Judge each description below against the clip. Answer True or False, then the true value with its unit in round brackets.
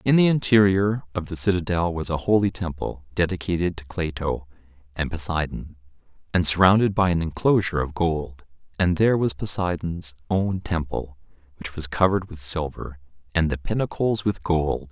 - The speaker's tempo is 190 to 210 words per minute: False (155 wpm)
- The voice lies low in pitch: True (85 Hz)